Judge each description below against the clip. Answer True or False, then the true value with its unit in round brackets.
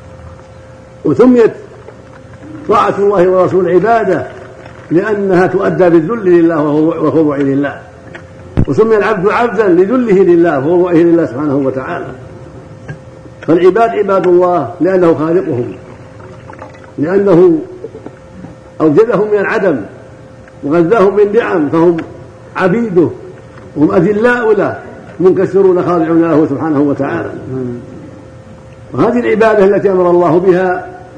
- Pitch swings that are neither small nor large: False (6.8 semitones)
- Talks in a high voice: False (170 Hz)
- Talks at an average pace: True (90 wpm)